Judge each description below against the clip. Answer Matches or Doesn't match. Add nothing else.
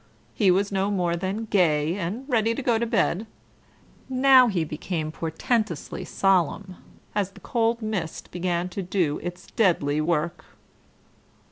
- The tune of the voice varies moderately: Matches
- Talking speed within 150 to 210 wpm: Doesn't match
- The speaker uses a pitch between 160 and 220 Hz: Matches